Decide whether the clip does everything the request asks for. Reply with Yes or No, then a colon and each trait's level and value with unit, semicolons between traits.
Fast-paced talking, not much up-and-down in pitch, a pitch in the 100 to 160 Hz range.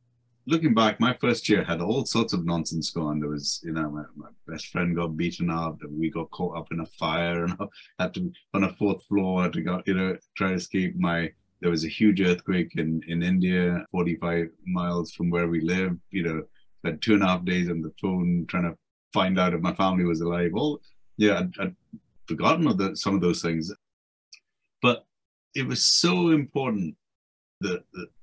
No: fast, 210 wpm; narrow, 2.3 semitones; very low, 90 Hz